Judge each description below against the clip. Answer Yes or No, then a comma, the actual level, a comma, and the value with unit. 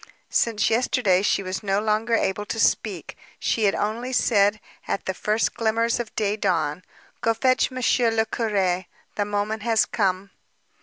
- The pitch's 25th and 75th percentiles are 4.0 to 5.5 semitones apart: No, narrow, 2.5 semitones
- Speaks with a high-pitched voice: Yes, high, 215 Hz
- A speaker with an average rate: Yes, average, 160 wpm